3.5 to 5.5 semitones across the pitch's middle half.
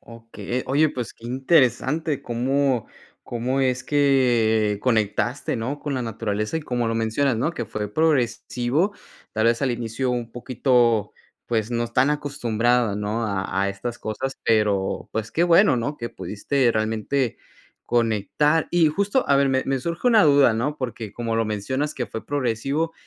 Yes: average, 3.8 semitones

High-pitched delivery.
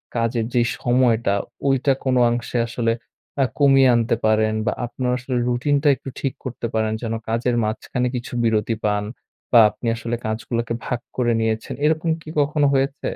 No: low, 120 Hz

